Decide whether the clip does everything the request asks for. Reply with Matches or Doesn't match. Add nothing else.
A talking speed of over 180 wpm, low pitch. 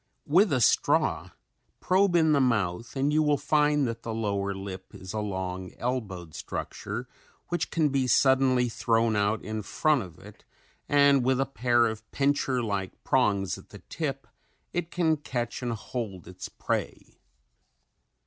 Doesn't match